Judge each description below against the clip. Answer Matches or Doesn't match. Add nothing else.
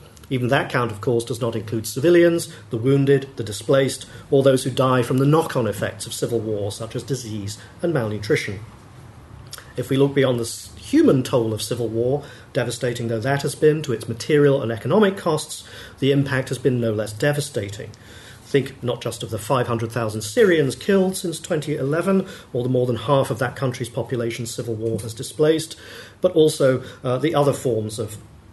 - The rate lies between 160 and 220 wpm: Matches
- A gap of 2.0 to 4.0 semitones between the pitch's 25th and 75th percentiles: Matches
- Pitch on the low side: Matches